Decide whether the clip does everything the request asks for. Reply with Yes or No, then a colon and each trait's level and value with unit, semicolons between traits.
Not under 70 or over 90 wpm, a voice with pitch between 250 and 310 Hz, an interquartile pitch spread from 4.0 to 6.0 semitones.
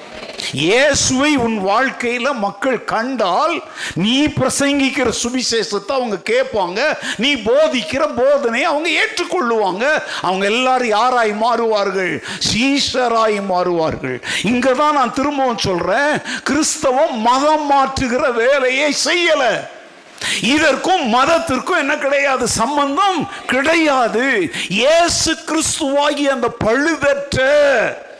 Yes: average, 85 wpm; very high, 270 Hz; average, 4.4 semitones